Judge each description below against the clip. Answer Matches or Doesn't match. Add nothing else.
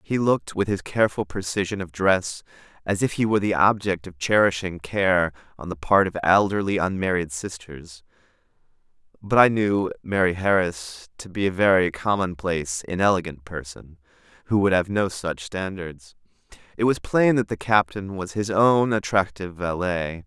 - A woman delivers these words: Doesn't match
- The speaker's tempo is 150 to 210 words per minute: Matches